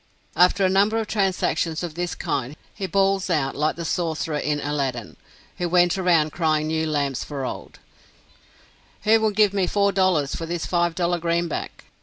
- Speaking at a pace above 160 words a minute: Yes, average, 175 wpm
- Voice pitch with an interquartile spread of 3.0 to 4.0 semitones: Yes, average, 3.7 semitones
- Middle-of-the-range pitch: Yes, medium, 170 Hz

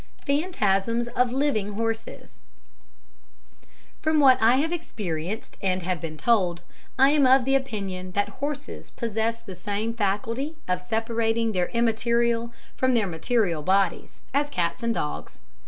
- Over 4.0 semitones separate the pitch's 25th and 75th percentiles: Yes, average, 4.8 semitones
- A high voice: Yes, high, 225 Hz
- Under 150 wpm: Yes, average, 140 wpm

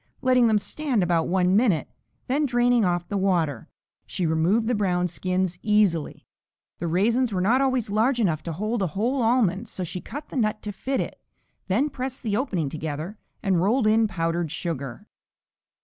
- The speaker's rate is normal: Yes, average, 180 wpm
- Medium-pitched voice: No, high, 200 Hz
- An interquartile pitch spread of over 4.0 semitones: Yes, wide, 5.4 semitones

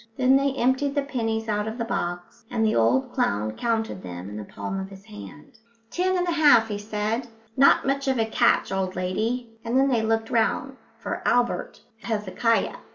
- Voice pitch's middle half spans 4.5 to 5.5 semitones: Yes, average, 5.1 semitones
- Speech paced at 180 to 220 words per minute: Yes, average, 195 wpm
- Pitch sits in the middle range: No, high, 225 Hz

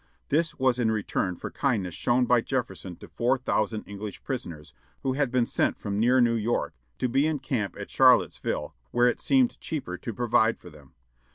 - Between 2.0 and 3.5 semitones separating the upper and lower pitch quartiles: No, average, 3.9 semitones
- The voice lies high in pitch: No, low, 120 Hz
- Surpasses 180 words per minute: Yes, average, 190 wpm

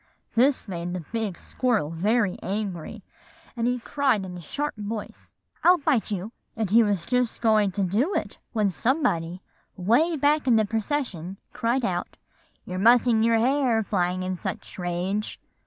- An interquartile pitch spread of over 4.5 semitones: Yes, average, 5.0 semitones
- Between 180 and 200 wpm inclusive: No, average, 165 wpm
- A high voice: Yes, high, 215 Hz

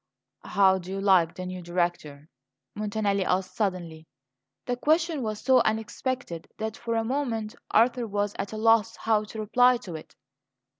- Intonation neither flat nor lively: Yes, average, 3.9 semitones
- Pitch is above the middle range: Yes, high, 215 Hz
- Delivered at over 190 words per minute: No, average, 160 wpm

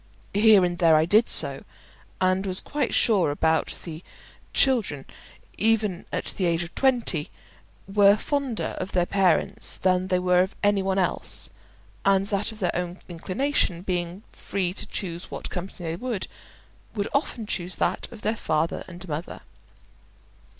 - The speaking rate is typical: Yes, average, 160 wpm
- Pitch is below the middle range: No, medium, 185 Hz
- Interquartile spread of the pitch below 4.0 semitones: Yes, average, 3.2 semitones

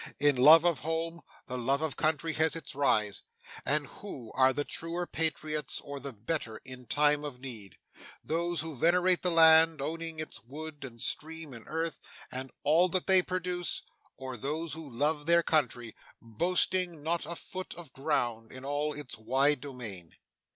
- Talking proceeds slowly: No, average, 170 wpm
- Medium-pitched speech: Yes, medium, 150 Hz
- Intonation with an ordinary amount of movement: Yes, average, 3.9 semitones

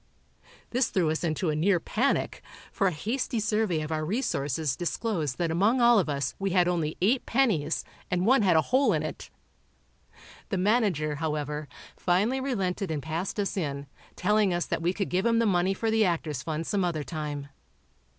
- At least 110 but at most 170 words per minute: No, average, 190 wpm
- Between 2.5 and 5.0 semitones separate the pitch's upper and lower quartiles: No, wide, 5.6 semitones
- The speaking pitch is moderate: Yes, medium, 180 Hz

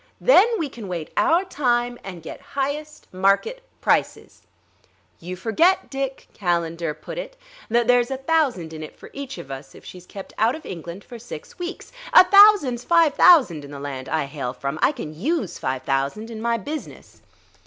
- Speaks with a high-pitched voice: Yes, high, 230 Hz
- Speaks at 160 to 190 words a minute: Yes, average, 185 wpm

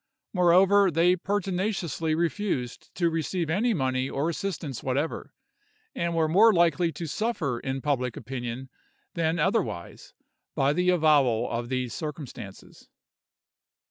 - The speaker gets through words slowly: Yes, slow, 120 wpm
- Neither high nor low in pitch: Yes, medium, 160 Hz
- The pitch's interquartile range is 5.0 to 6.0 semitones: Yes, average, 5.3 semitones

